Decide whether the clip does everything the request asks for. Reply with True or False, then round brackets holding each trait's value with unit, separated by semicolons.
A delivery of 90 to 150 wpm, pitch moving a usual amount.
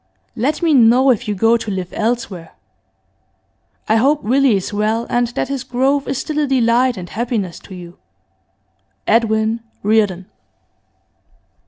True (145 wpm; 3.7 semitones)